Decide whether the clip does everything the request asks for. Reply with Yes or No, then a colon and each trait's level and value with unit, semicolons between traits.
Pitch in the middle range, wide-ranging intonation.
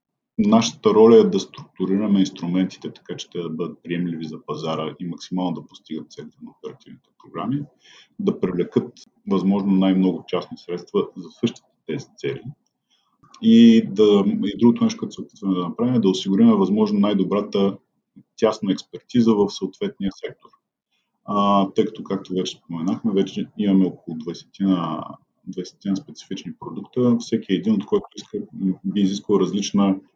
No: low, 100 Hz; wide, 7.6 semitones